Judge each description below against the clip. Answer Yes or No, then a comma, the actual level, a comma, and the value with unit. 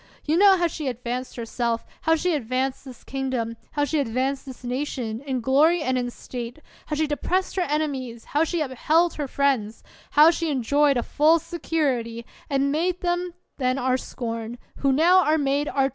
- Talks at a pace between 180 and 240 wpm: Yes, average, 185 wpm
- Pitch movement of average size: Yes, average, 3.9 semitones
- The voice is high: Yes, very high, 275 Hz